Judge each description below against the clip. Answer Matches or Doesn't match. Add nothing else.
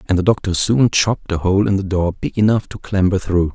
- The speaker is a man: Matches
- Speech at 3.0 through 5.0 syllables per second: Doesn't match